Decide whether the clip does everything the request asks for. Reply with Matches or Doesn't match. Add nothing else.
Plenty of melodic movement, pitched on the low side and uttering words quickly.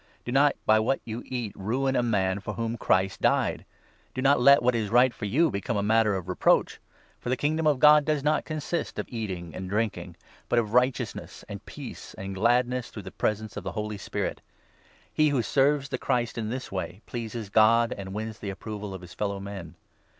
Doesn't match